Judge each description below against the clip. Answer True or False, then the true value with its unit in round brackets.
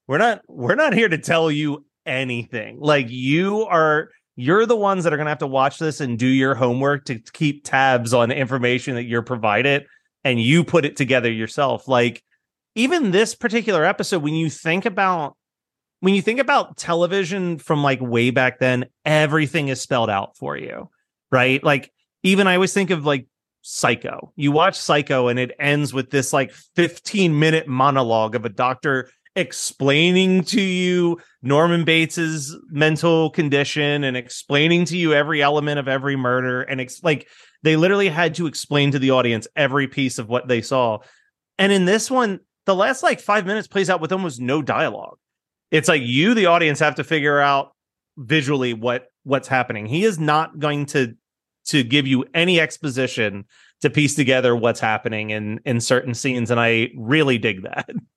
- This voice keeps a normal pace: True (180 wpm)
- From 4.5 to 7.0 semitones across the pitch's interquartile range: True (4.9 semitones)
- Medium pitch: True (145 Hz)